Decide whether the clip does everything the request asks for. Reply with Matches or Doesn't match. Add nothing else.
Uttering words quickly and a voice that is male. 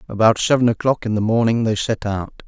Matches